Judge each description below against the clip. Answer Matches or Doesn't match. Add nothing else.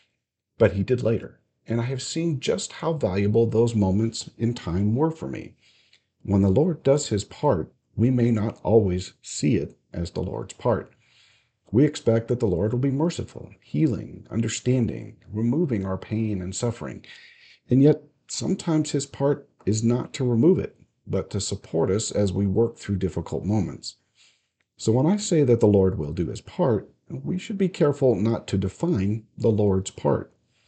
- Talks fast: Doesn't match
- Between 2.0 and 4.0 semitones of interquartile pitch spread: Doesn't match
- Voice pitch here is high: Doesn't match